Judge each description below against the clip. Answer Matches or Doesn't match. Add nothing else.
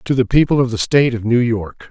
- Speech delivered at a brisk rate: Matches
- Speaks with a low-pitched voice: Matches